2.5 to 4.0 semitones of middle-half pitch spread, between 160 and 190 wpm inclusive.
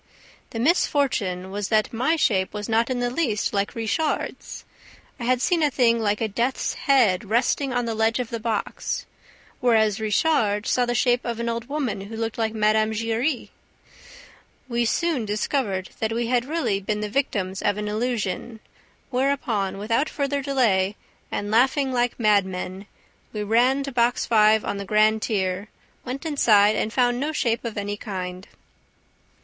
Yes: average, 3.2 semitones; average, 165 wpm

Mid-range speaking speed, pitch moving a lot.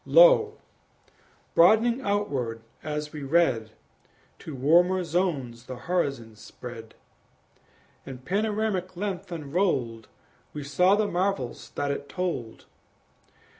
No: slow, 100 wpm; wide, 6.8 semitones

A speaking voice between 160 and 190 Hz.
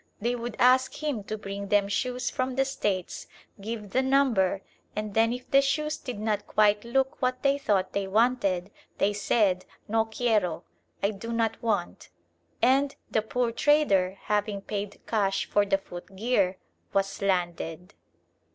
No: high, 215 Hz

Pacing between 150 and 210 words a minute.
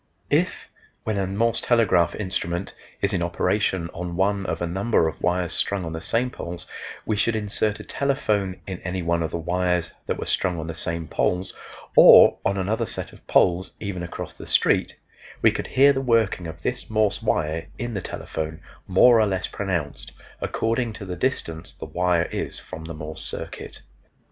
Yes: average, 190 wpm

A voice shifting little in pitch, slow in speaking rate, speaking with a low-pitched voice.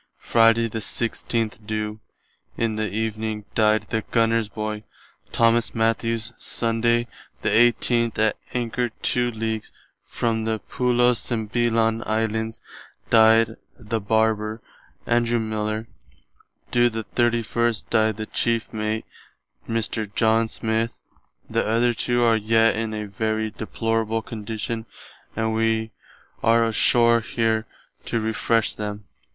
Yes: narrow, 1.0 semitones; slow, 125 wpm; low, 110 Hz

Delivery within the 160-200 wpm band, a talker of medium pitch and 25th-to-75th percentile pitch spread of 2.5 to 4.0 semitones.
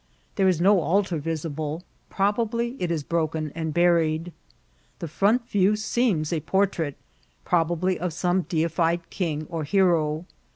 No: slow, 135 wpm; medium, 170 Hz; average, 3.4 semitones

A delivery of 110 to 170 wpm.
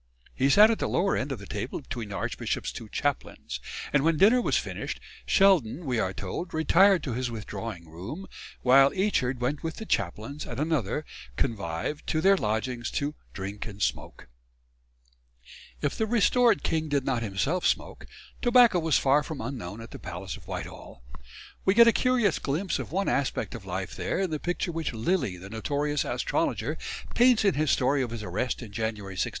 No: average, 185 wpm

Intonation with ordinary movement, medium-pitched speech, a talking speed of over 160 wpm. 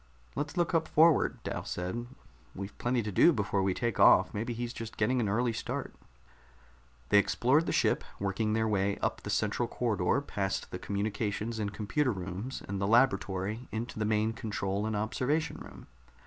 No: average, 3.3 semitones; low, 110 Hz; average, 175 wpm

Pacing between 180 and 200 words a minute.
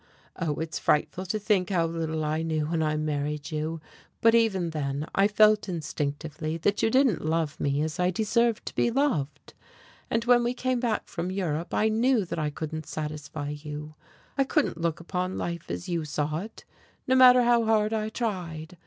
Yes: average, 190 wpm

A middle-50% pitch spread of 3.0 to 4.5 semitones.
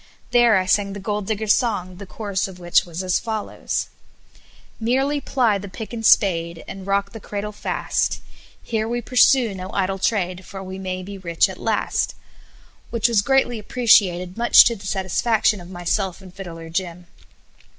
Yes: average, 3.3 semitones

